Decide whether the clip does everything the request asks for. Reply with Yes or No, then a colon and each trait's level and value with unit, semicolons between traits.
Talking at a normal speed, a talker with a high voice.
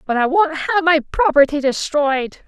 Yes: average, 170 wpm; very high, 300 Hz